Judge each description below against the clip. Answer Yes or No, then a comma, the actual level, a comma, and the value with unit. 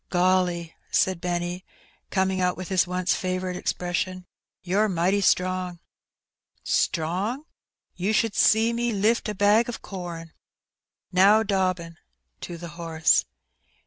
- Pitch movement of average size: No, narrow, 2.3 semitones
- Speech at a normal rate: No, slow, 120 wpm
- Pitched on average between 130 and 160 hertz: No, medium, 185 Hz